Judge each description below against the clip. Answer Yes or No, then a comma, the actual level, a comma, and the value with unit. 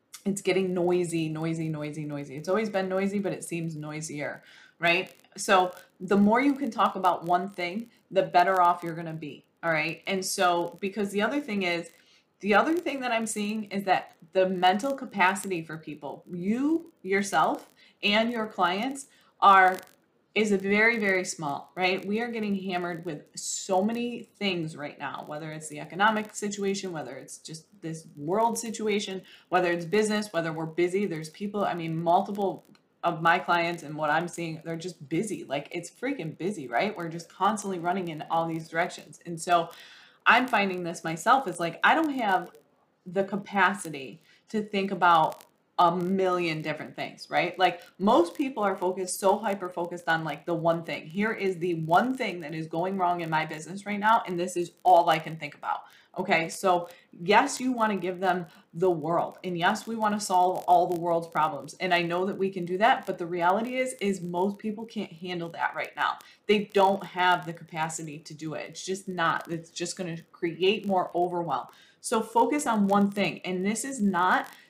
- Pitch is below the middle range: No, medium, 180 Hz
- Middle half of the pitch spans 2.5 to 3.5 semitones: Yes, average, 3.1 semitones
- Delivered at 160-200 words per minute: Yes, average, 195 wpm